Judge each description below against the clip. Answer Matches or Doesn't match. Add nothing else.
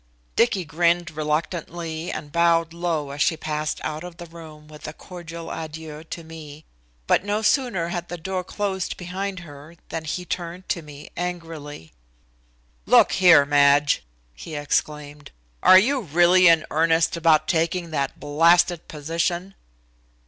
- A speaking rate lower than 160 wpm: Matches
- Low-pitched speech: Doesn't match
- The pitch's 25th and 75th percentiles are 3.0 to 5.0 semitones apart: Doesn't match